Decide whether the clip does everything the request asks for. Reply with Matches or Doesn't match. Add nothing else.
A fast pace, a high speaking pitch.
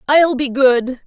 Doesn't match